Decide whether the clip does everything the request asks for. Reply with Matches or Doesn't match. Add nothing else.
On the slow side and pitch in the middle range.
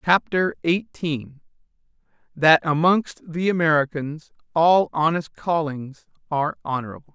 Matches